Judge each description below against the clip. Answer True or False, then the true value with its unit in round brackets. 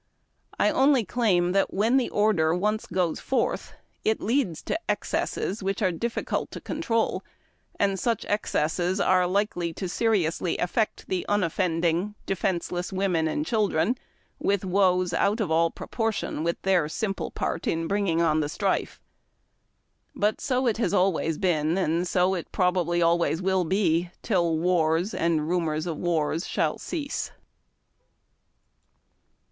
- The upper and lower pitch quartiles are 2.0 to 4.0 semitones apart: True (3.6 semitones)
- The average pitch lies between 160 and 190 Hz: True (185 Hz)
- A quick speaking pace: False (140 wpm)